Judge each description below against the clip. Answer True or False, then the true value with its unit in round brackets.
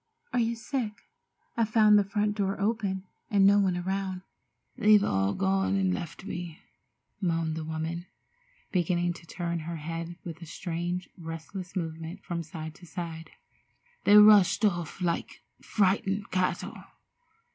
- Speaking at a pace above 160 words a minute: False (145 wpm)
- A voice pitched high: False (180 Hz)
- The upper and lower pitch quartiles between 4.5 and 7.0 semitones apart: False (3.2 semitones)